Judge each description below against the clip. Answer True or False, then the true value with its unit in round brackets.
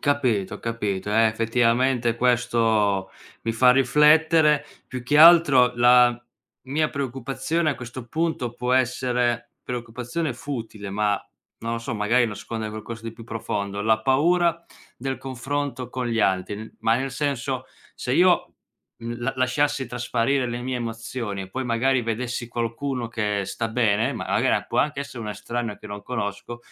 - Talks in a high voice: False (120 Hz)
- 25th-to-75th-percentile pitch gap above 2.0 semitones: True (2.7 semitones)